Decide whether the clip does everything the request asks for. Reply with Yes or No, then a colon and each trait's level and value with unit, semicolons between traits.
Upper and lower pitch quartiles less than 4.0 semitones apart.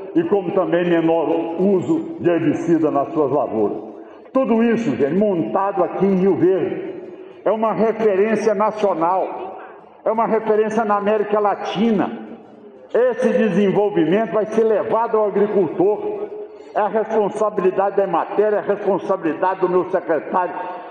Yes: average, 3.3 semitones